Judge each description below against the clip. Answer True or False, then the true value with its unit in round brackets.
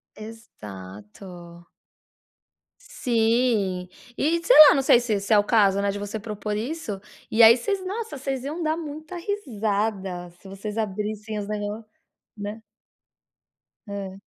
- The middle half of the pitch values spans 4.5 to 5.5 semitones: True (4.9 semitones)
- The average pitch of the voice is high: True (215 Hz)